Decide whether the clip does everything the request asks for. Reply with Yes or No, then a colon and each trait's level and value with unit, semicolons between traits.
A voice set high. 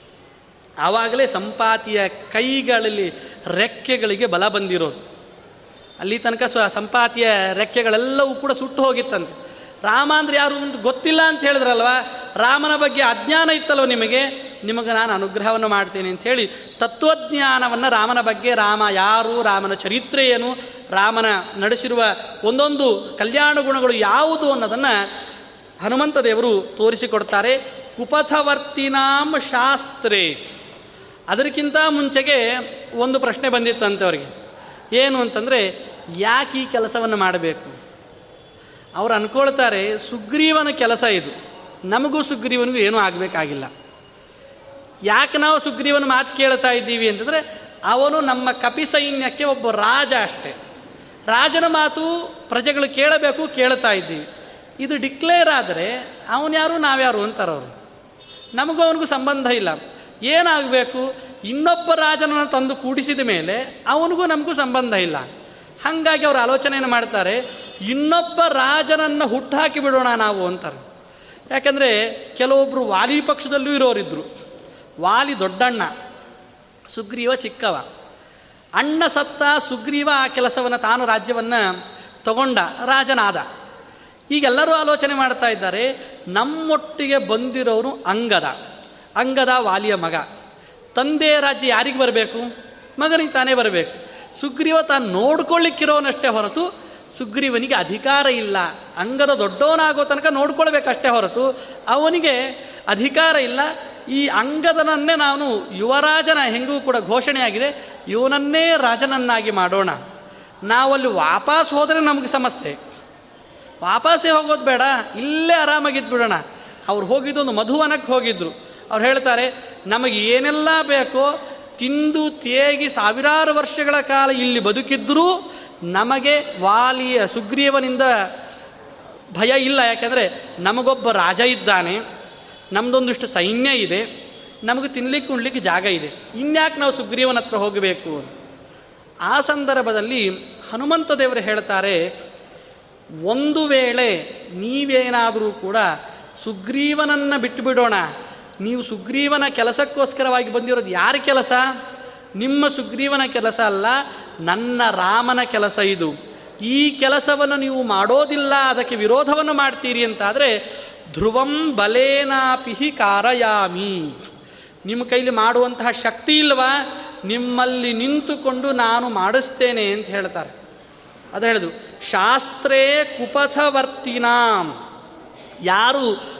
Yes: very high, 260 Hz